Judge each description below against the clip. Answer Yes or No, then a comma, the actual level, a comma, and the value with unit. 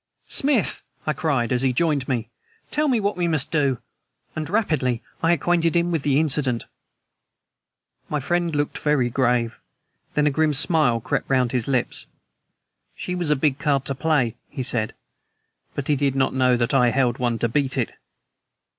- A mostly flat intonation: No, average, 4.2 semitones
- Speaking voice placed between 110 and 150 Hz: Yes, medium, 140 Hz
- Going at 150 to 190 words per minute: Yes, average, 175 wpm